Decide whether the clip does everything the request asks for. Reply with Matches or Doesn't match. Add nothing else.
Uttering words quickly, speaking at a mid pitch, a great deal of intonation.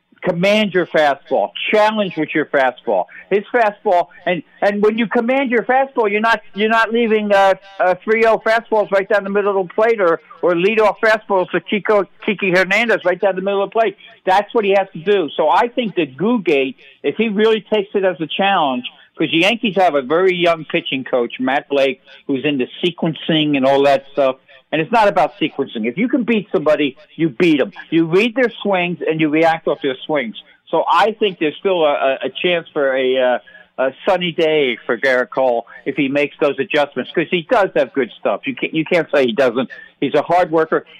Matches